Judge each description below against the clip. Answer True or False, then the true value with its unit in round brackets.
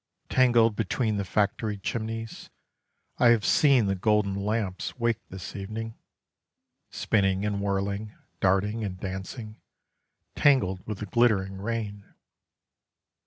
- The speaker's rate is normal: False (115 wpm)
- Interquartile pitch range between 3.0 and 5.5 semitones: False (2.6 semitones)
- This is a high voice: False (105 Hz)